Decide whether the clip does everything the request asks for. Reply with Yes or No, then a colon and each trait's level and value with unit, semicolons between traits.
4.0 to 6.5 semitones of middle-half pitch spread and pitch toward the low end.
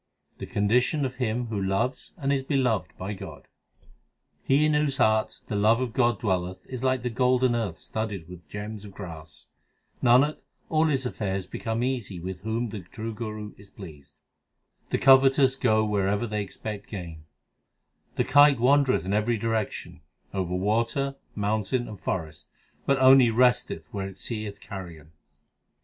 Yes: average, 4.7 semitones; low, 110 Hz